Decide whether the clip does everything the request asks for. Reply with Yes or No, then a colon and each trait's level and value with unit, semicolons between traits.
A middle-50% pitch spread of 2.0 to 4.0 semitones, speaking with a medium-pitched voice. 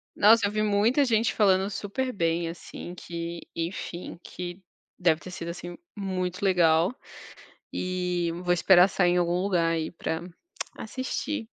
Yes: average, 3.0 semitones; medium, 180 Hz